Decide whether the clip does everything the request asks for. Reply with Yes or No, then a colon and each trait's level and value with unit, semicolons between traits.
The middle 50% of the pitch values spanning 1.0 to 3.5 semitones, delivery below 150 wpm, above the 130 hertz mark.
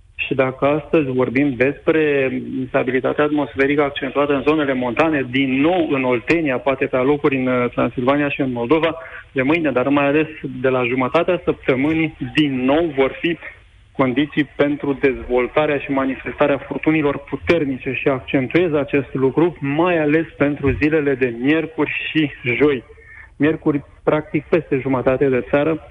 Yes: narrow, 2.5 semitones; average, 140 wpm; medium, 140 Hz